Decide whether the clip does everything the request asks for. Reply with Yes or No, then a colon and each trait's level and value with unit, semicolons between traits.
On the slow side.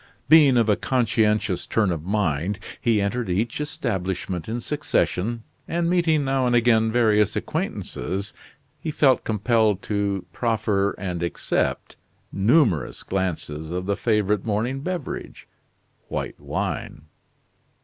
Yes: slow, 120 wpm